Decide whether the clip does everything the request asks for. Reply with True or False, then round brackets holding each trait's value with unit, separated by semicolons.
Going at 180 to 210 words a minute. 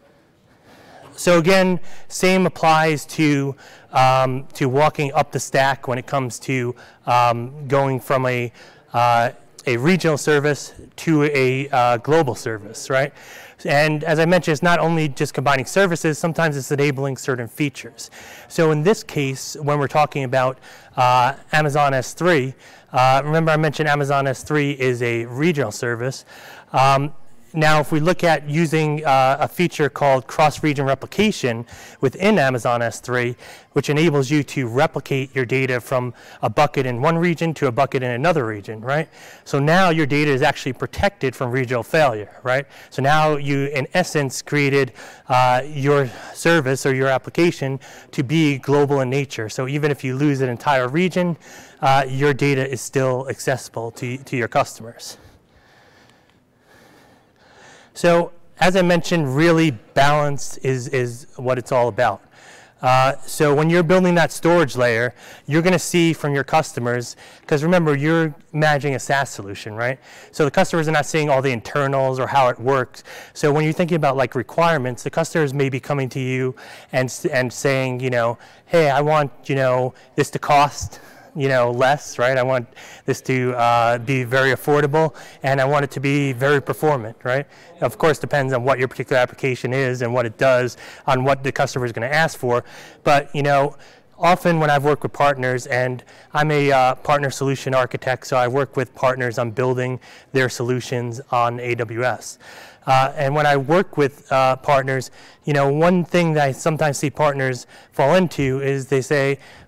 False (170 wpm)